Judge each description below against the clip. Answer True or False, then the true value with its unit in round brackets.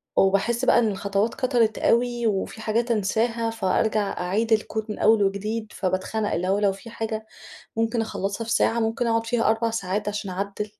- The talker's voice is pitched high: True (220 Hz)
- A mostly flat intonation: True (2.3 semitones)